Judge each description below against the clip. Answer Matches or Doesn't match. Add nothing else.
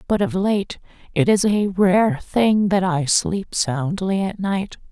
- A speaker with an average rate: Matches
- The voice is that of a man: Doesn't match